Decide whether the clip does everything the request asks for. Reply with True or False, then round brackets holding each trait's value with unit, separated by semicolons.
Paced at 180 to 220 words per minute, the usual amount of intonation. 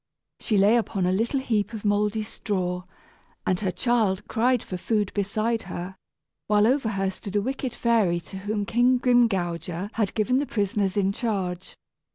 False (170 wpm; 3.4 semitones)